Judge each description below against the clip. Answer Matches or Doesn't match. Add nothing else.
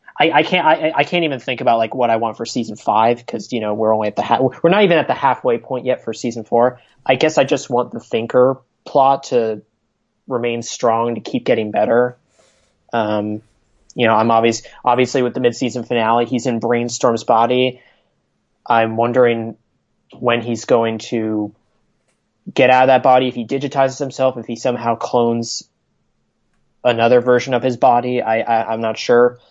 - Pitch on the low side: Matches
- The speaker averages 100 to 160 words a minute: Doesn't match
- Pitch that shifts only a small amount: Matches